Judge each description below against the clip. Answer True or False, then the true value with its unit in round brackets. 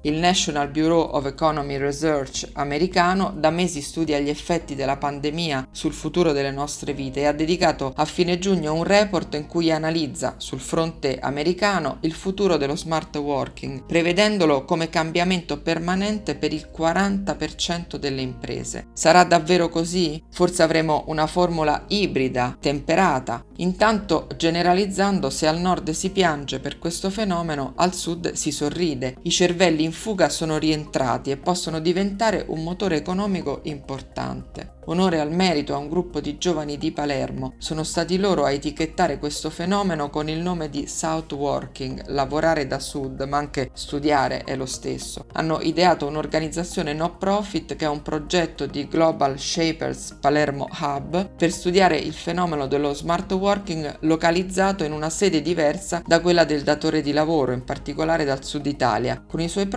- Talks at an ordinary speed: True (155 wpm)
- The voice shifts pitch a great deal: False (3.3 semitones)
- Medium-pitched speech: True (160 Hz)